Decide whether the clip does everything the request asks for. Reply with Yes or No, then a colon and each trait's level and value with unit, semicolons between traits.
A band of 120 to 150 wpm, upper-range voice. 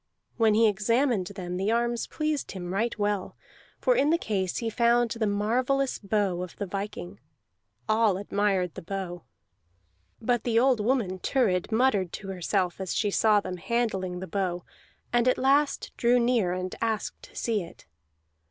No: average, 165 wpm; high, 210 Hz